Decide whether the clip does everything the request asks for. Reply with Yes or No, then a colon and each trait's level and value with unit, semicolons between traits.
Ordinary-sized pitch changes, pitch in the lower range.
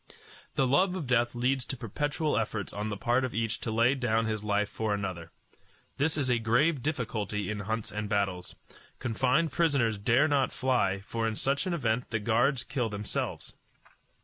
Yes: average, 4.0 semitones; low, 115 Hz